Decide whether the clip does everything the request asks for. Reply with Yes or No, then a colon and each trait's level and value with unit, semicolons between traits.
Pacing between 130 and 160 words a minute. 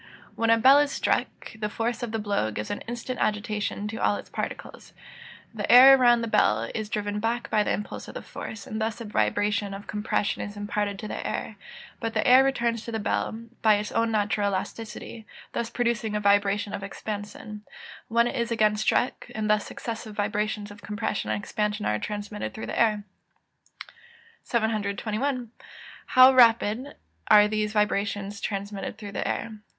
No: average, 180 wpm